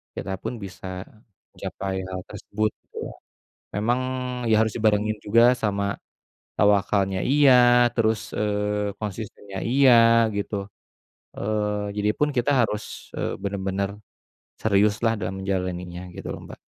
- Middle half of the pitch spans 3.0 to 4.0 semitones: No, narrow, 2.5 semitones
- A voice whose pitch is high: No, low, 105 Hz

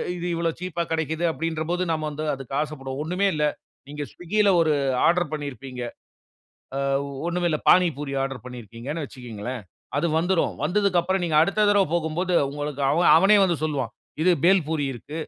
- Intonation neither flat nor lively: Yes, average, 3.8 semitones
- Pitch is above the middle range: No, medium, 160 Hz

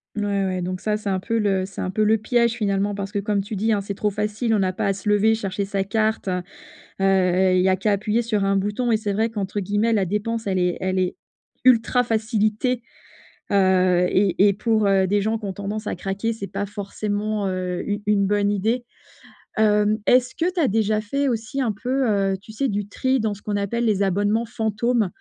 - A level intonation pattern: Yes, narrow, 2.2 semitones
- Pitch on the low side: No, high, 205 Hz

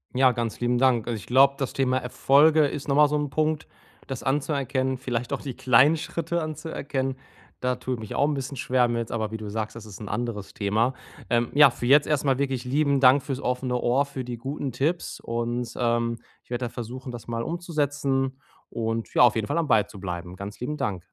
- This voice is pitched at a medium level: No, low, 130 Hz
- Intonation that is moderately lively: Yes, average, 3.1 semitones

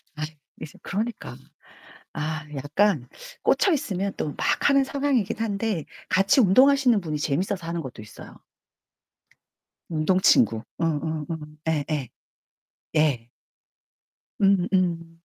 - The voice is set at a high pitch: No, medium, 170 Hz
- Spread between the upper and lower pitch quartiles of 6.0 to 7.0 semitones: No, wide, 5.4 semitones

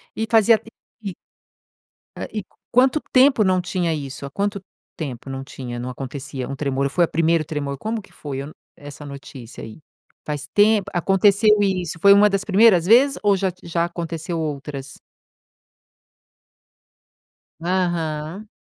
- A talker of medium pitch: Yes, medium, 170 Hz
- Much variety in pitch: Yes, wide, 6.1 semitones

